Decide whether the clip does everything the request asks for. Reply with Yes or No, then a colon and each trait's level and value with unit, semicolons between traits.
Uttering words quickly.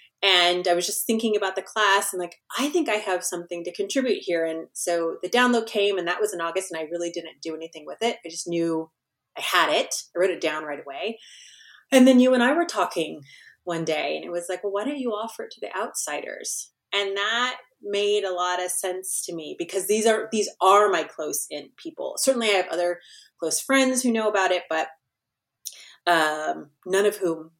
Yes: fast, 225 wpm